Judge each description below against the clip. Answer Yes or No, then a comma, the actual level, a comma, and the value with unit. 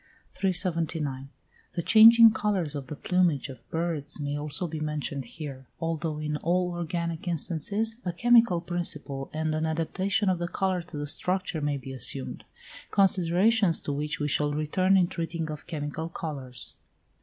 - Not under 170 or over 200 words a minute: No, average, 155 wpm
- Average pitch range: Yes, average, 3.6 semitones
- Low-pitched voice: No, medium, 165 Hz